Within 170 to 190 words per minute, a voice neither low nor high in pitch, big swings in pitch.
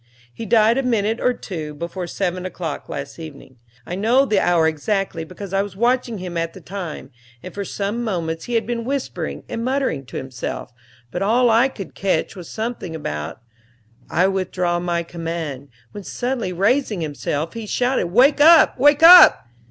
No: average, 175 wpm; high, 195 Hz; wide, 5.9 semitones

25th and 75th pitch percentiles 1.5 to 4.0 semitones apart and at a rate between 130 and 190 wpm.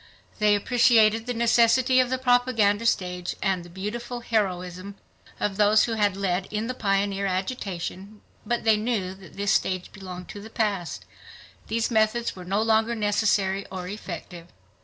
Yes: average, 3.2 semitones; average, 160 wpm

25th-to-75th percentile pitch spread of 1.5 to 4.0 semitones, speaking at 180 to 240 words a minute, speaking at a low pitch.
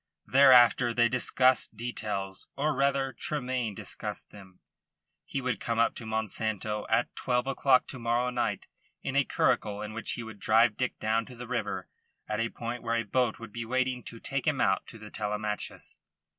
Yes: average, 2.8 semitones; average, 185 wpm; low, 115 Hz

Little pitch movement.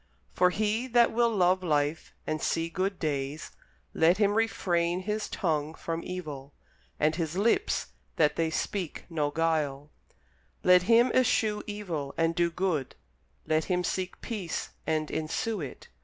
No: average, 4.6 semitones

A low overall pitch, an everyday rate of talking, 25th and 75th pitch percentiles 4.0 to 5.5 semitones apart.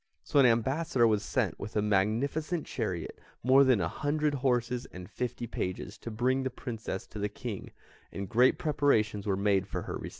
Yes: low, 120 Hz; average, 190 wpm; average, 4.3 semitones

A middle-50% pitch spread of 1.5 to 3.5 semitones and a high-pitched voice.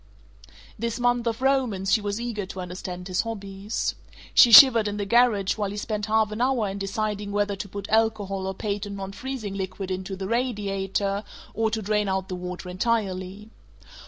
Yes: narrow, 2.6 semitones; high, 205 Hz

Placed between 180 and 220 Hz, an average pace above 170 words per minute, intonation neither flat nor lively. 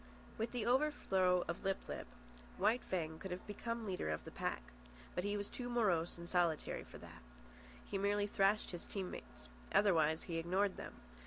Yes: high, 190 Hz; average, 180 wpm; average, 3.4 semitones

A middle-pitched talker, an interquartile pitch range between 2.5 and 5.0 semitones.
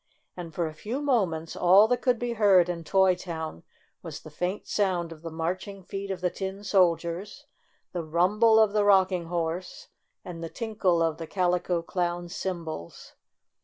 Yes: medium, 180 Hz; average, 3.0 semitones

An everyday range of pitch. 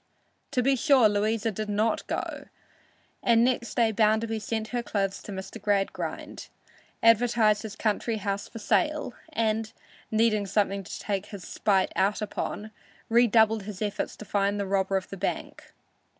No: narrow, 2.1 semitones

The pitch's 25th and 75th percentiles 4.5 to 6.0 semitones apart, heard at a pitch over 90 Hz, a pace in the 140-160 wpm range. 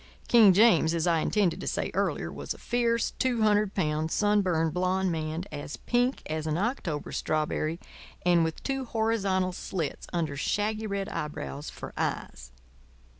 Yes: average, 5.2 semitones; medium, 185 Hz; average, 155 wpm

